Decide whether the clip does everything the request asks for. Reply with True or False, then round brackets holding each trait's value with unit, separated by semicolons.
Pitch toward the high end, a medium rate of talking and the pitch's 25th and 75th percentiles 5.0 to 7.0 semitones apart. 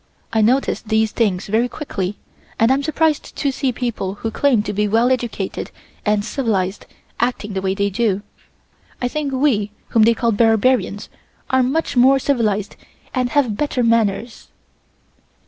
False (230 Hz; 155 wpm; 3.8 semitones)